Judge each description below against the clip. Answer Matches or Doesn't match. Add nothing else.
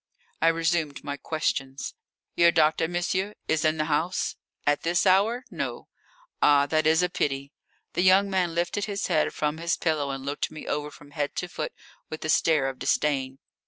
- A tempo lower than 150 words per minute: Doesn't match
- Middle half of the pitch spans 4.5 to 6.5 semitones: Doesn't match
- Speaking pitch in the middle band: Matches